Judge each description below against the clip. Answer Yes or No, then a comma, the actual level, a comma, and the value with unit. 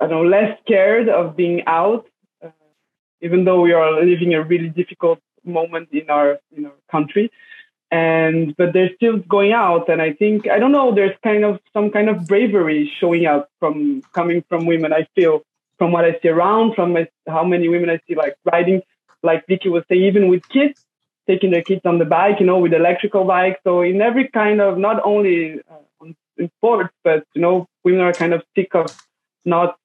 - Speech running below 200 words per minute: No, fast, 205 wpm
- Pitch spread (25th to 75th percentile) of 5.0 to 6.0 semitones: No, average, 3.6 semitones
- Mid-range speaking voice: Yes, medium, 180 Hz